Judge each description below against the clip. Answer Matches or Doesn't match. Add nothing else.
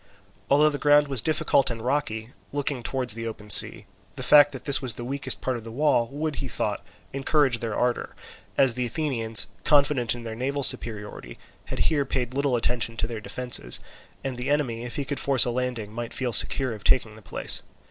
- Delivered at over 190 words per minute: Matches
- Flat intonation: Doesn't match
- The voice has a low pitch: Matches